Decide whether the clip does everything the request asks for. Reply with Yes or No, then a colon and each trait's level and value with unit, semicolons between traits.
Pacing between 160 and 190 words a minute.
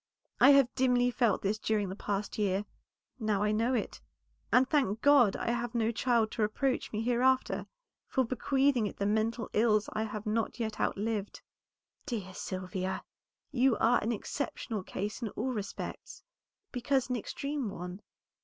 Yes: average, 165 wpm